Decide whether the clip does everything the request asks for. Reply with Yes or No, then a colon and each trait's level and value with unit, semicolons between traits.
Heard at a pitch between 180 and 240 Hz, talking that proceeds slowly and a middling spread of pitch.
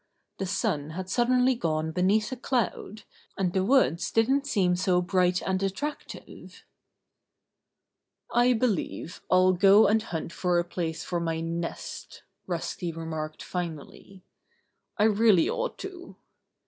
Yes: medium, 185 Hz; slow, 130 wpm; average, 4.6 semitones